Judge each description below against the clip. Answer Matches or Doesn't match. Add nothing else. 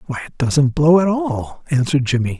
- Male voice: Matches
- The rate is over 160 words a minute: Matches